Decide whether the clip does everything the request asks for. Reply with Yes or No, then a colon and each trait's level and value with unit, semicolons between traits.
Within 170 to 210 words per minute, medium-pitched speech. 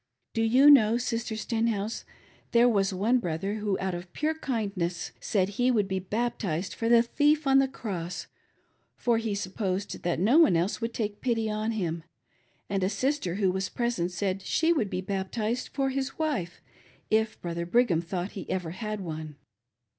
No: average, 180 wpm; high, 210 Hz